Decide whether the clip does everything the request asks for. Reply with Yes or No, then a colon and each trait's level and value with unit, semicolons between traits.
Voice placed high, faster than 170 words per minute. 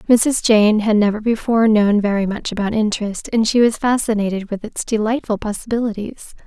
No: high, 215 Hz; average, 165 wpm